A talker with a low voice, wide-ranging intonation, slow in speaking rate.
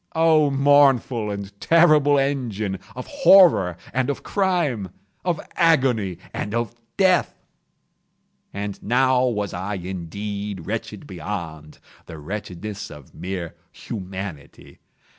Yes: low, 105 Hz; wide, 6.7 semitones; slow, 105 wpm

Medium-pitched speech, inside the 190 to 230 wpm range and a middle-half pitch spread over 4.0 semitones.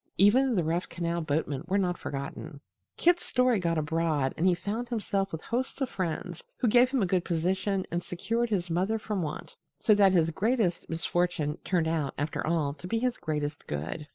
Yes: medium, 180 Hz; average, 195 wpm; average, 4.7 semitones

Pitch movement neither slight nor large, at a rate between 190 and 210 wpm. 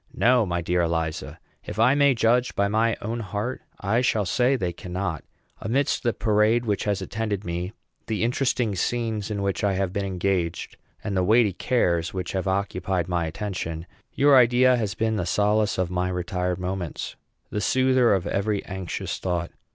No: average, 4.0 semitones; average, 175 wpm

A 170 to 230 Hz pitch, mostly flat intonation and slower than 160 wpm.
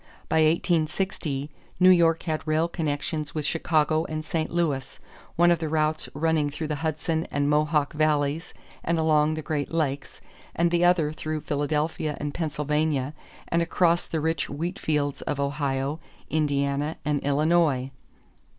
No: medium, 155 Hz; narrow, 1.9 semitones; average, 145 wpm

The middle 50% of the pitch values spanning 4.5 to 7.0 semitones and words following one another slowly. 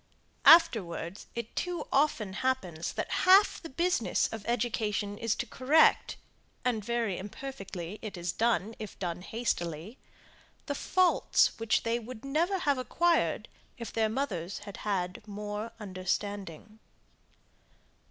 Yes: average, 5.1 semitones; slow, 125 wpm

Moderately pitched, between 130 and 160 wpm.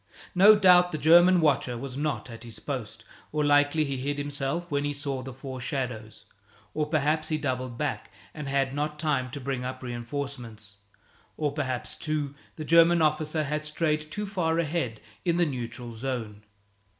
No: medium, 145 Hz; average, 175 wpm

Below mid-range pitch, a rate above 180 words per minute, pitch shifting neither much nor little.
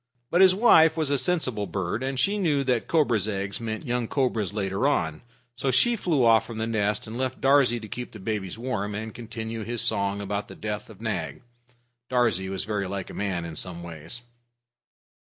Yes: low, 110 Hz; average, 200 wpm; average, 4.5 semitones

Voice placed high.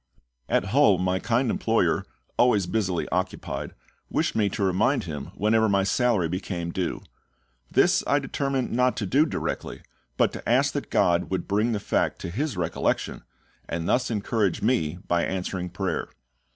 No: low, 100 Hz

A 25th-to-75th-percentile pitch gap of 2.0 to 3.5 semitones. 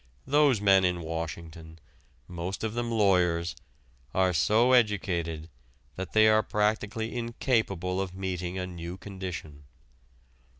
No: average, 4.2 semitones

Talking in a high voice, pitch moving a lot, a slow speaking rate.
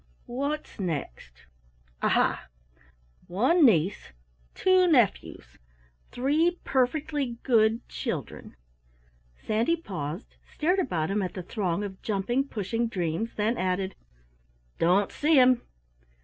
Yes: high, 225 Hz; wide, 6.7 semitones; slow, 105 wpm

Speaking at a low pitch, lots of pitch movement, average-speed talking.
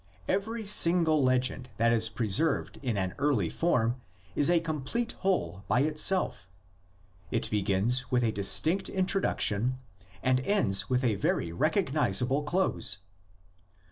No: low, 130 Hz; wide, 7.1 semitones; slow, 130 wpm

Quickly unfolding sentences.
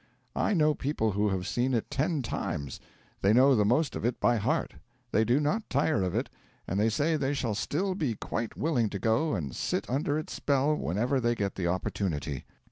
Yes: fast, 210 wpm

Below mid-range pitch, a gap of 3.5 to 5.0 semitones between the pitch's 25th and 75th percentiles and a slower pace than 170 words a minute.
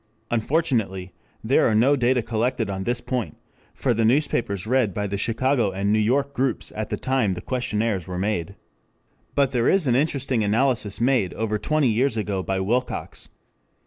No: low, 115 Hz; average, 4.2 semitones; average, 175 wpm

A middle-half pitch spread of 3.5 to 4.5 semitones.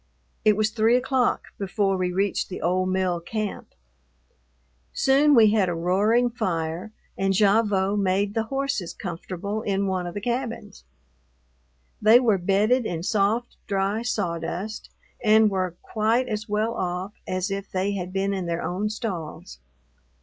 No: average, 2.9 semitones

